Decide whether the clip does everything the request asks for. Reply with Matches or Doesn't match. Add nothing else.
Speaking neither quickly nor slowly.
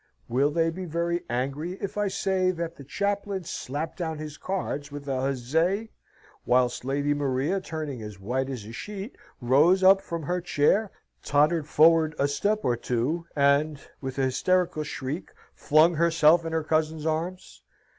Matches